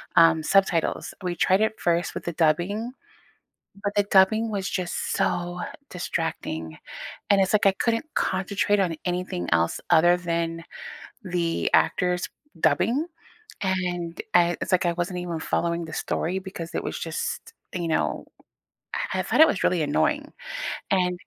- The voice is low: No, medium, 175 Hz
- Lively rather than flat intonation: No, narrow, 2.4 semitones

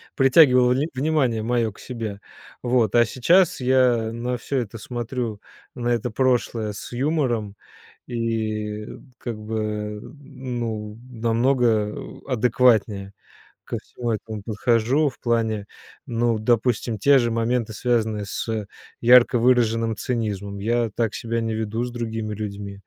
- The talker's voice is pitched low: Yes, low, 115 Hz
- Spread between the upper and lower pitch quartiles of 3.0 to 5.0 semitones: No, narrow, 2.4 semitones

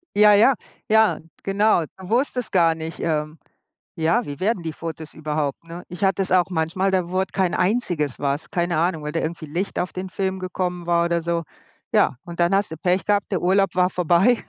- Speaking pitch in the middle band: Yes, medium, 180 Hz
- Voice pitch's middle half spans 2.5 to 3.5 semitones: Yes, average, 2.8 semitones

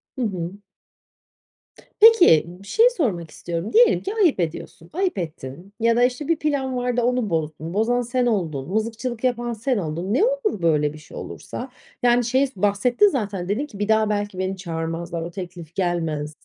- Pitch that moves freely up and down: Yes, wide, 6.6 semitones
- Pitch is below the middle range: No, high, 210 Hz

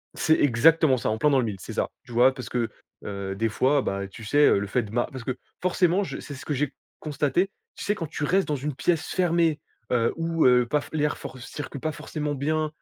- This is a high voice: No, medium, 140 Hz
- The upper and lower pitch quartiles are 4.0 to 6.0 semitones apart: Yes, average, 4.5 semitones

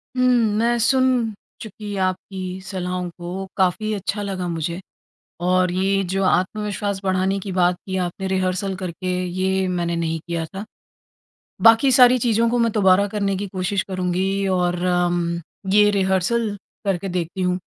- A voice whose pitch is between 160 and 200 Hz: Yes, high, 190 Hz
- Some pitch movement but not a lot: No, narrow, 2.2 semitones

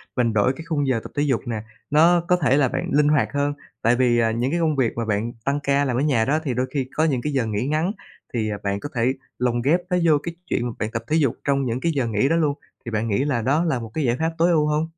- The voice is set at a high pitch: No, low, 135 Hz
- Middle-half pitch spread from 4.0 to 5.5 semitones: Yes, average, 4.3 semitones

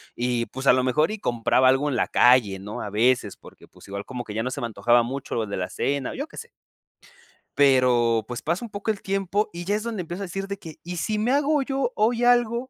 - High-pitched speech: No, medium, 140 Hz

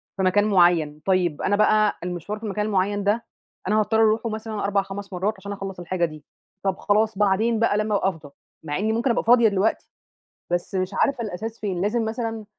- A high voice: Yes, high, 205 Hz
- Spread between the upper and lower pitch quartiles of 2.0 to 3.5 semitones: Yes, average, 2.7 semitones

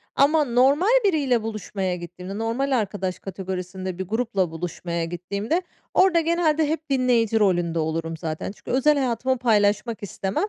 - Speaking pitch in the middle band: No, high, 215 Hz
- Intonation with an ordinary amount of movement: No, wide, 6.8 semitones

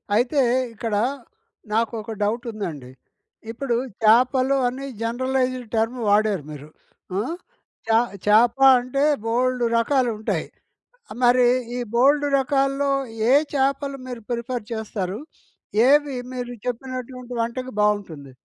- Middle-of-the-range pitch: No, high, 245 Hz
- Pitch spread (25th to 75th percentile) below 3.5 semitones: Yes, average, 2.9 semitones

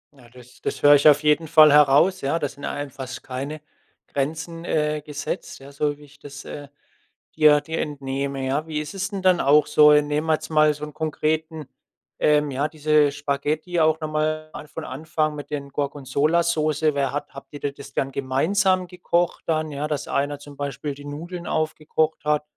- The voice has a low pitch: No, medium, 150 Hz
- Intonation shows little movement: Yes, narrow, 1.7 semitones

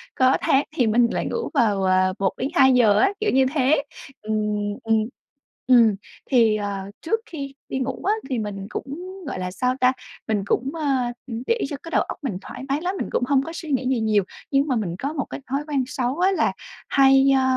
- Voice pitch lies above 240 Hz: Yes, very high, 260 Hz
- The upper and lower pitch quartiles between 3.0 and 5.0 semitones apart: Yes, average, 4.7 semitones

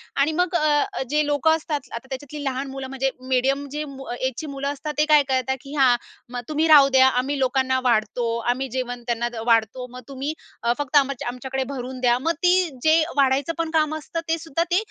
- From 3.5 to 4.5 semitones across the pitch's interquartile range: No, average, 2.9 semitones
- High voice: Yes, very high, 270 Hz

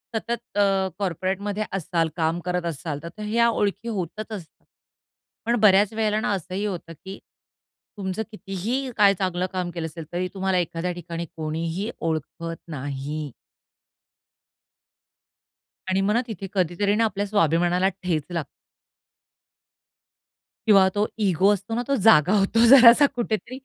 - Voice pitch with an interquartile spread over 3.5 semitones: Yes, average, 3.9 semitones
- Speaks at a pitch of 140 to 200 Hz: Yes, high, 190 Hz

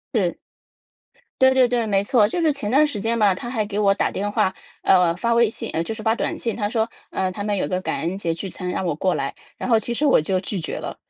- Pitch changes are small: No, average, 3.9 semitones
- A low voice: No, high, 205 Hz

